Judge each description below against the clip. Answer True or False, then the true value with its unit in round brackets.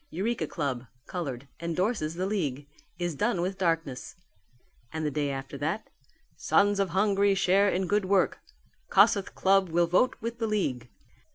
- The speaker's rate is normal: True (155 wpm)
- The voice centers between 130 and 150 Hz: False (180 Hz)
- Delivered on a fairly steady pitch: False (4.6 semitones)